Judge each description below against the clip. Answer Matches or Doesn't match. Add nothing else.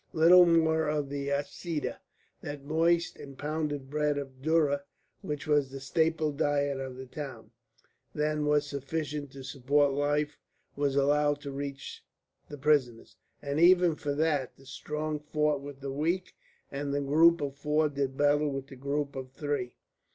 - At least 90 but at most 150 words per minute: Doesn't match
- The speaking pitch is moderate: Matches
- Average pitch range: Doesn't match